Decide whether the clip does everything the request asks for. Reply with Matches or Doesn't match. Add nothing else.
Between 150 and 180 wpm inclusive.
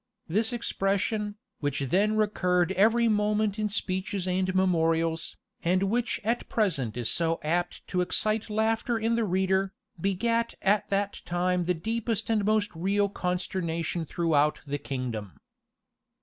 Doesn't match